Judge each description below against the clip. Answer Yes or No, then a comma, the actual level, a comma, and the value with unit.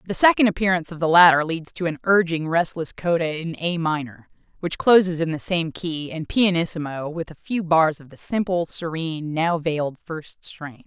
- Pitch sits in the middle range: Yes, medium, 165 Hz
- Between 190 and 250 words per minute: Yes, average, 195 wpm